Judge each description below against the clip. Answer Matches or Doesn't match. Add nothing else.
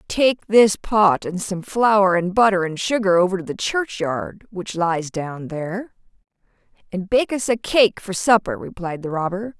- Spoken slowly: Doesn't match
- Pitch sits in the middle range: Doesn't match